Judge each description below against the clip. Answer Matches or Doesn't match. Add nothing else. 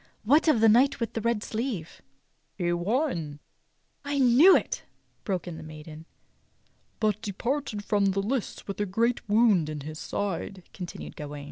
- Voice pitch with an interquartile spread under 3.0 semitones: Doesn't match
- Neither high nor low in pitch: Doesn't match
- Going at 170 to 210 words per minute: Matches